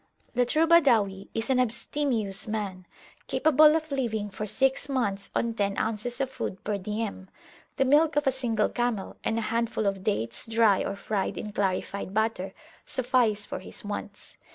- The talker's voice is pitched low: No, high, 225 Hz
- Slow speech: No, average, 170 wpm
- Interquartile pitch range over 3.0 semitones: Yes, average, 4.3 semitones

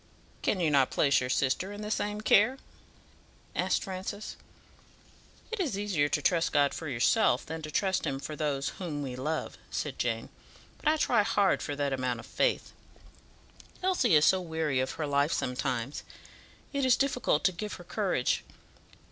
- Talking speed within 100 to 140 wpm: No, average, 175 wpm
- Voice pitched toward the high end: No, medium, 160 Hz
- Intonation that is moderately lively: No, wide, 6.5 semitones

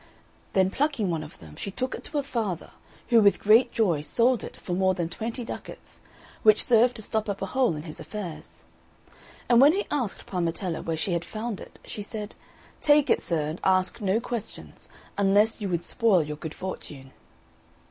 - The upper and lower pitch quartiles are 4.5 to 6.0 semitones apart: Yes, average, 5.2 semitones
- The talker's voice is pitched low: No, high, 200 Hz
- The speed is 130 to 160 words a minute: No, average, 195 wpm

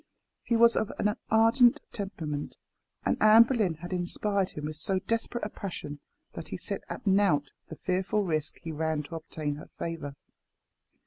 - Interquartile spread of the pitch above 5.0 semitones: Yes, wide, 5.4 semitones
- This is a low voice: No, medium, 185 Hz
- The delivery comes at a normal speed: Yes, average, 170 wpm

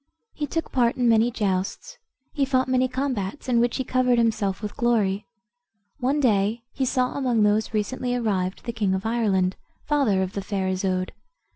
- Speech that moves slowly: No, average, 175 wpm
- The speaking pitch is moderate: No, high, 230 Hz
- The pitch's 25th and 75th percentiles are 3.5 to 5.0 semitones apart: Yes, average, 4.4 semitones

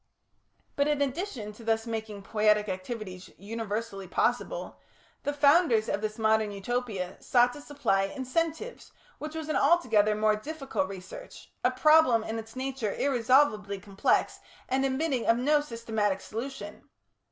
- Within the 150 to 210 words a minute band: No, average, 140 wpm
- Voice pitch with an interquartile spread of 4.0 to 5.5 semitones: Yes, average, 5.1 semitones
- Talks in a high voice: Yes, high, 230 Hz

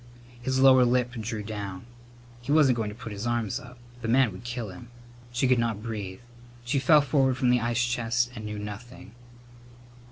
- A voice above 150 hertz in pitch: No, low, 120 Hz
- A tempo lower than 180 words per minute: No, average, 190 wpm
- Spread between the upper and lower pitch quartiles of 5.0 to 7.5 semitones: No, average, 2.7 semitones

